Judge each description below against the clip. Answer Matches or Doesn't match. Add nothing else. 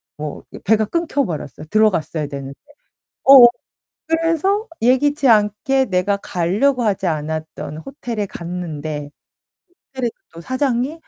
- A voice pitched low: Doesn't match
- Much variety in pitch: Matches